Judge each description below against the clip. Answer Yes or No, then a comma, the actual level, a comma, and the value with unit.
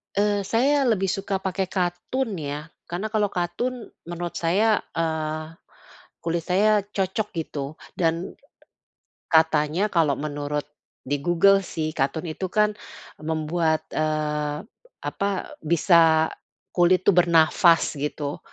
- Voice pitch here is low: No, medium, 170 Hz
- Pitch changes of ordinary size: Yes, average, 4.0 semitones